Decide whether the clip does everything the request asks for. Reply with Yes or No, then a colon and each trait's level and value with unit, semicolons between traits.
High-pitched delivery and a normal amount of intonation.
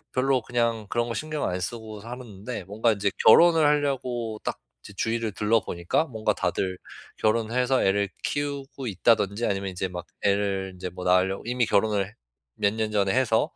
No: low, 110 Hz; average, 3.8 semitones